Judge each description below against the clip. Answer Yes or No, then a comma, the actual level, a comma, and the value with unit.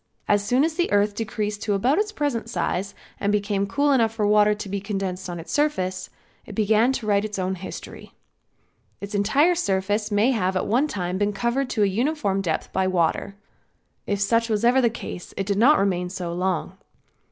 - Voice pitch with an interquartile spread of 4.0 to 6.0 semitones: No, average, 3.5 semitones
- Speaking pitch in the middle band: No, high, 205 Hz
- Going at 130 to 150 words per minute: No, average, 200 wpm